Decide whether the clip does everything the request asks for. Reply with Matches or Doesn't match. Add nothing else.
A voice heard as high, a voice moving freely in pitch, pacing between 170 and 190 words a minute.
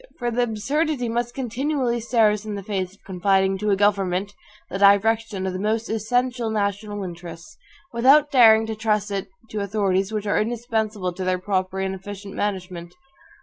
Doesn't match